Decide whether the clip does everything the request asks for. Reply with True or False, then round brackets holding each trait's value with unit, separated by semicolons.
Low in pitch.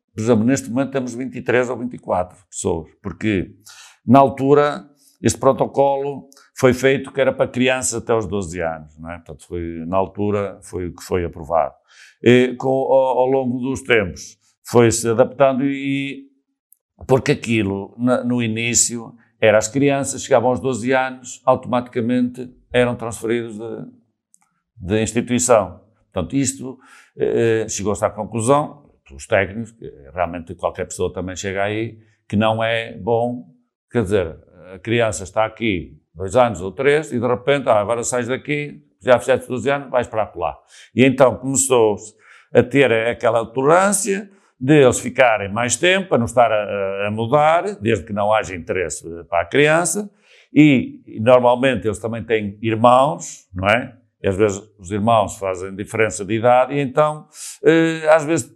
True (120 Hz)